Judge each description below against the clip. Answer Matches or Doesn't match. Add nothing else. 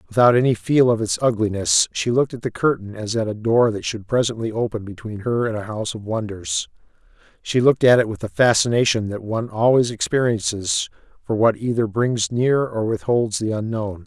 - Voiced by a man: Matches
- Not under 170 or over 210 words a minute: Matches